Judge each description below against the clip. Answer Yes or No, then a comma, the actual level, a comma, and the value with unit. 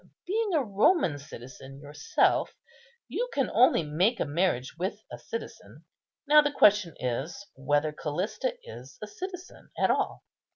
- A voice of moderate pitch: No, high, 195 Hz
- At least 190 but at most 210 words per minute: No, average, 140 wpm